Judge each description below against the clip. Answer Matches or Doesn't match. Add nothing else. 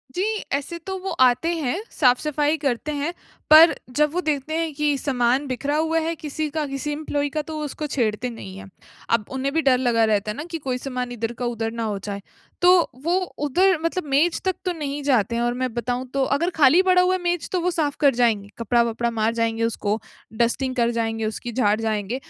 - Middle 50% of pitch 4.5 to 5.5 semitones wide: Matches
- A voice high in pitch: Matches